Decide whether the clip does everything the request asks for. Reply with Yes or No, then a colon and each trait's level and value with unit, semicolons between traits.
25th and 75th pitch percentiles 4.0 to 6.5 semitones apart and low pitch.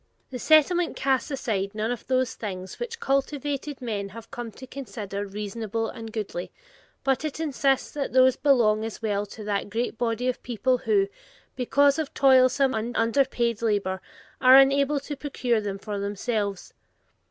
No: average, 4.3 semitones; high, 240 Hz